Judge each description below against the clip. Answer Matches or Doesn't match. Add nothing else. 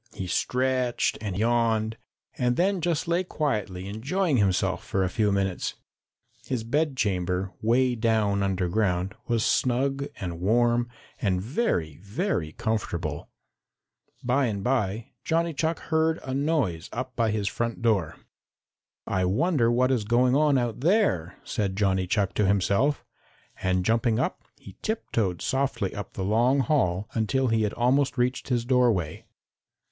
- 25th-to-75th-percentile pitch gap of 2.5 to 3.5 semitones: Doesn't match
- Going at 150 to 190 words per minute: Doesn't match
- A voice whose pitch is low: Matches